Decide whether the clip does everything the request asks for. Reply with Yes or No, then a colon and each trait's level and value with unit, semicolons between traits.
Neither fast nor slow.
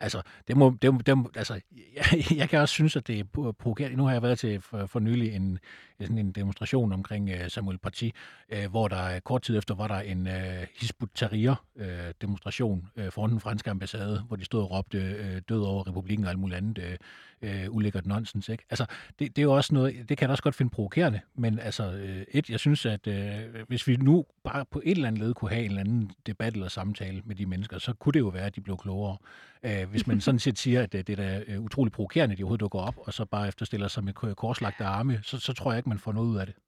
No: fast, 240 wpm